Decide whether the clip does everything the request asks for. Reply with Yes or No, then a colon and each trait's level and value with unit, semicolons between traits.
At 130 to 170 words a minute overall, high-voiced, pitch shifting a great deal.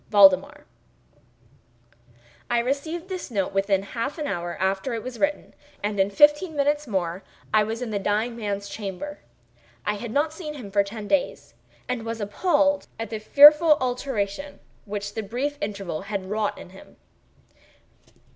Yes: average, 155 wpm; high, 220 Hz; wide, 6.1 semitones